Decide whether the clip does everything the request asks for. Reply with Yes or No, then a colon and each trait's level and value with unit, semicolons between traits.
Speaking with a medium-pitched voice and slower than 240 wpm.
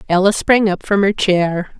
No: high, 195 Hz; average, 200 wpm